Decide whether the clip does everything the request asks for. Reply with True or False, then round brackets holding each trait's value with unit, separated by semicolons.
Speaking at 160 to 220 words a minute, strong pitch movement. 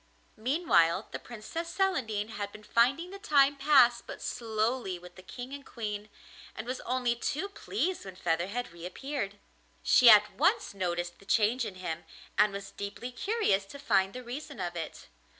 True (170 wpm; 5.9 semitones)